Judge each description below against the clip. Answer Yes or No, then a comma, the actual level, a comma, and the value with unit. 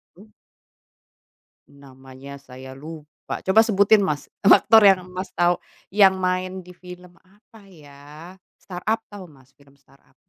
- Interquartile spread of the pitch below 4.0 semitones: No, average, 5.3 semitones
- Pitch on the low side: No, medium, 180 Hz